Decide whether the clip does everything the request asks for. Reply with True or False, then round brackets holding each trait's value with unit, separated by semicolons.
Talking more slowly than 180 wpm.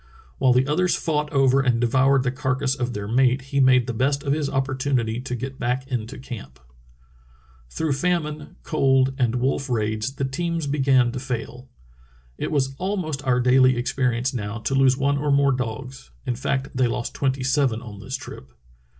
False (185 wpm)